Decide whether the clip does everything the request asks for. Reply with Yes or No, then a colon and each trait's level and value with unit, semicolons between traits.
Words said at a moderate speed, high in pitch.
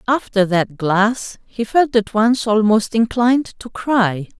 Yes: average, 150 wpm; high, 220 Hz